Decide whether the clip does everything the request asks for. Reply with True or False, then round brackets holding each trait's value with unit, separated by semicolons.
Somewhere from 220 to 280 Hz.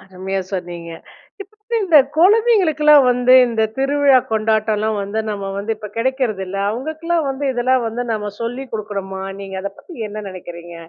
True (225 Hz)